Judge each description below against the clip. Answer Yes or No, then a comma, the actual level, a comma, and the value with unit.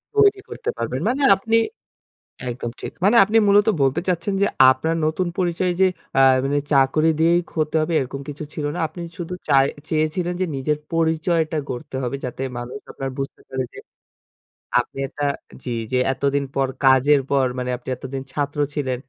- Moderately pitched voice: Yes, medium, 150 Hz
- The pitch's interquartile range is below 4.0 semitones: No, average, 4.4 semitones